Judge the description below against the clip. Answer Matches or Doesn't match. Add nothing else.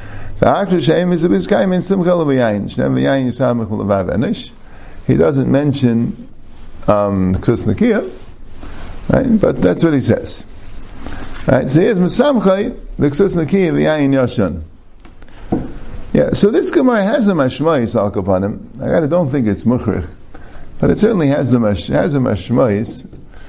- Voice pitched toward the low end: Matches